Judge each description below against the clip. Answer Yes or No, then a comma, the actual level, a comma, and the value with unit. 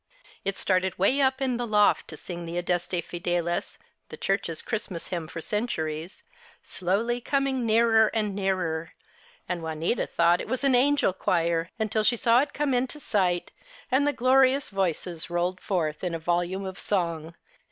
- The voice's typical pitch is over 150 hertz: Yes, high, 190 Hz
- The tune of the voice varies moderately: No, wide, 5.7 semitones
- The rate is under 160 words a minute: No, average, 165 wpm